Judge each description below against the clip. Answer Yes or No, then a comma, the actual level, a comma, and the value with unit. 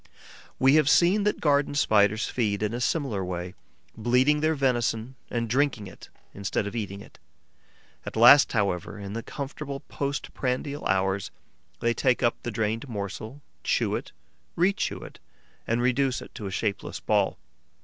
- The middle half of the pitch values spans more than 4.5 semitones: Yes, average, 5.3 semitones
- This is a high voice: No, low, 120 Hz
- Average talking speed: Yes, average, 160 wpm